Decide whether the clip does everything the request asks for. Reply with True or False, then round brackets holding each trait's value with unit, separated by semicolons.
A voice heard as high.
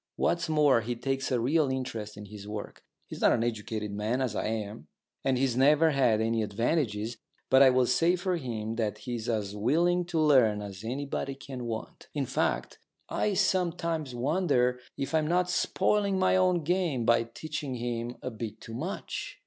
False (125 Hz)